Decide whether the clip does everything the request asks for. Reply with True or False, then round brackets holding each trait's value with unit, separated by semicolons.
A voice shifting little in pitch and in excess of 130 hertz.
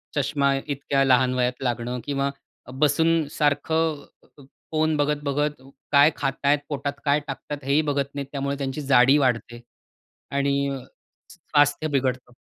True (1.6 semitones; 140 Hz)